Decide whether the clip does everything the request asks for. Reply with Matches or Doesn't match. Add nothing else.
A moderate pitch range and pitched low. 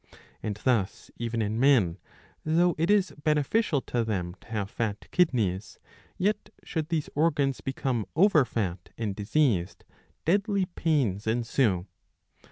Doesn't match